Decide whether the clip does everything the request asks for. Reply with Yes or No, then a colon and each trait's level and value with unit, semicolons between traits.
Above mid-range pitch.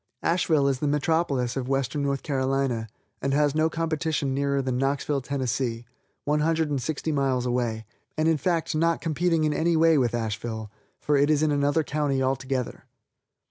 No: medium, 140 Hz